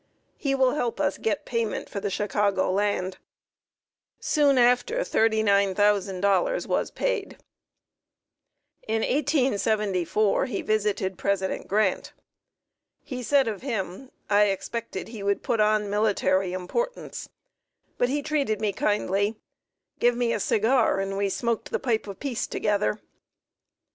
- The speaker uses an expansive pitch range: No, average, 3.6 semitones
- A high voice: Yes, high, 215 Hz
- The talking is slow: Yes, slow, 125 wpm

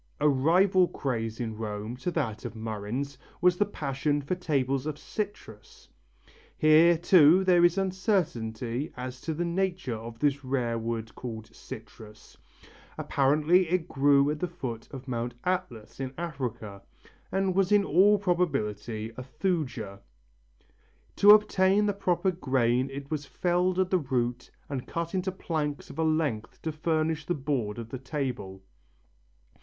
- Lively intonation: Yes, wide, 6.8 semitones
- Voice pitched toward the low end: No, medium, 145 Hz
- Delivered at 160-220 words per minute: No, average, 150 wpm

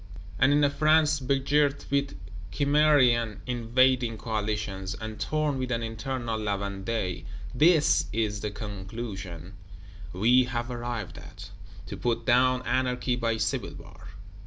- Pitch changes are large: No, average, 3.8 semitones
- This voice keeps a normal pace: No, slow, 130 wpm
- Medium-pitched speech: No, low, 120 Hz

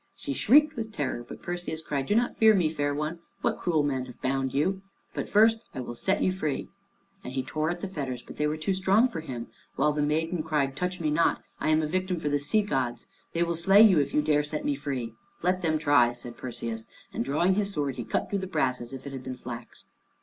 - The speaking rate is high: Yes, fast, 250 wpm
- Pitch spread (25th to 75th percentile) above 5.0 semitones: Yes, wide, 5.4 semitones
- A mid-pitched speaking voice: Yes, medium, 150 Hz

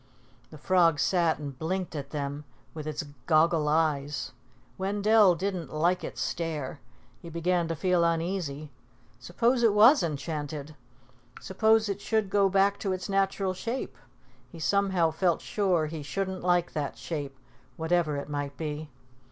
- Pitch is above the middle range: No, medium, 170 Hz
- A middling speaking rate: Yes, average, 145 wpm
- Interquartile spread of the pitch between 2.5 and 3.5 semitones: No, average, 4.2 semitones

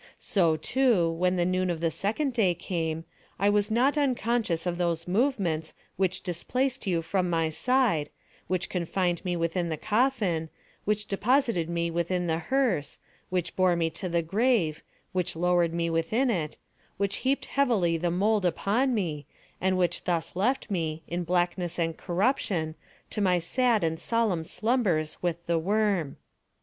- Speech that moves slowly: No, average, 160 wpm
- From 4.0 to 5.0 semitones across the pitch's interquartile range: Yes, average, 4.4 semitones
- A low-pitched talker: No, medium, 180 Hz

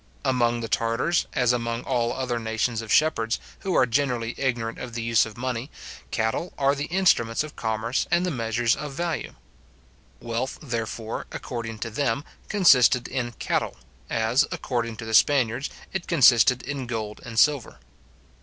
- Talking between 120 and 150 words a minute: No, average, 160 wpm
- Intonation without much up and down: No, average, 3.3 semitones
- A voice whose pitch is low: Yes, low, 120 Hz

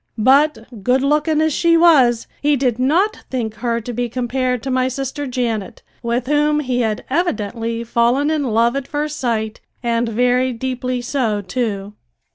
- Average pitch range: Yes, average, 3.4 semitones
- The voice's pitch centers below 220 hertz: No, very high, 250 Hz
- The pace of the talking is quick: No, average, 165 wpm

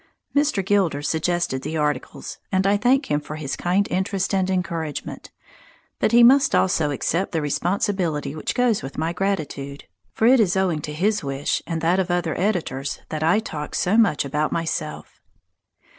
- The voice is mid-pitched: Yes, medium, 175 Hz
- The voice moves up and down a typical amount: Yes, average, 4.8 semitones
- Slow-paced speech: No, average, 175 wpm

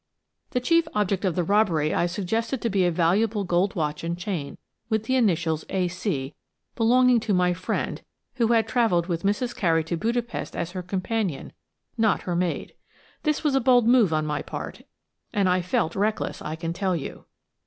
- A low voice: No, high, 190 Hz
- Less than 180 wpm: No, average, 185 wpm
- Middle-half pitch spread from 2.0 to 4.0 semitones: No, average, 4.9 semitones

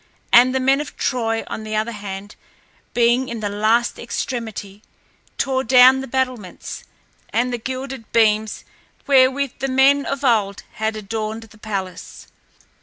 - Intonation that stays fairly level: No, average, 3.3 semitones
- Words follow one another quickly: No, average, 145 wpm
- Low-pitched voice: No, high, 235 Hz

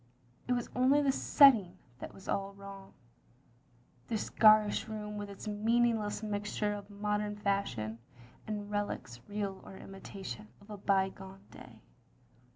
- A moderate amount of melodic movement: No, narrow, 1.6 semitones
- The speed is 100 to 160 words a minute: Yes, average, 140 wpm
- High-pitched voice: Yes, high, 205 Hz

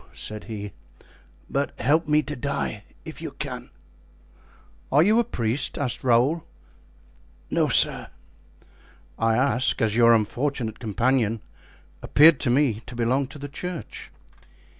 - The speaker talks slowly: Yes, slow, 130 wpm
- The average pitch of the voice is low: Yes, low, 125 Hz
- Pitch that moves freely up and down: No, average, 4.1 semitones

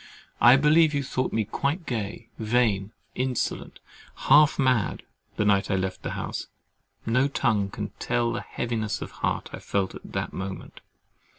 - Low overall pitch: Yes, low, 120 Hz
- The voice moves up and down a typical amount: Yes, average, 4.5 semitones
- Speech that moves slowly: No, average, 155 wpm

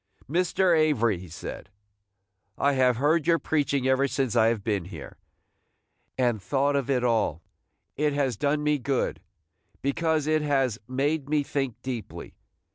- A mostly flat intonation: No, average, 3.8 semitones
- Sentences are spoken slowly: No, average, 150 wpm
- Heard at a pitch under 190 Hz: Yes, low, 135 Hz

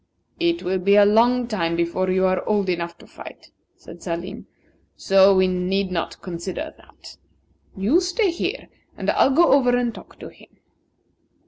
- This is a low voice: No, high, 195 Hz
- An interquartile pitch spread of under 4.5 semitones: No, average, 5.2 semitones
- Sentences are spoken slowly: No, average, 165 wpm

